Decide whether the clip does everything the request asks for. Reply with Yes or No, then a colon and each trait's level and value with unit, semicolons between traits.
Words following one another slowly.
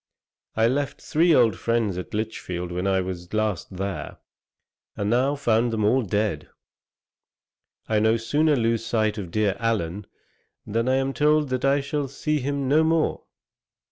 No: average, 160 wpm